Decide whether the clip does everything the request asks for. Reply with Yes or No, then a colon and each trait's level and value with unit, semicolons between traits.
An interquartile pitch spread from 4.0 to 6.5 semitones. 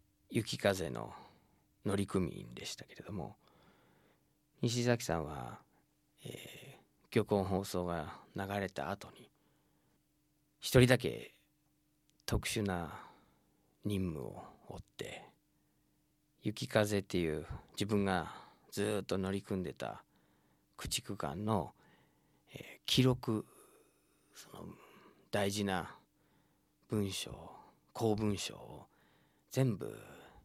Yes: wide, 5.4 semitones